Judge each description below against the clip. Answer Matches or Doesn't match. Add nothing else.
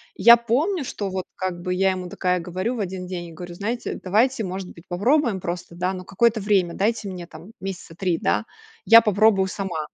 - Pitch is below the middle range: Doesn't match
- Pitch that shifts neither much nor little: Matches